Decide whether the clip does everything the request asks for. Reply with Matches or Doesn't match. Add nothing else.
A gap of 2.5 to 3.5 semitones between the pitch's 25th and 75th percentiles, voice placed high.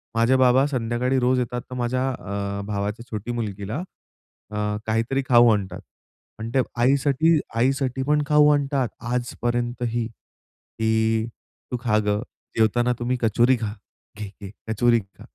Doesn't match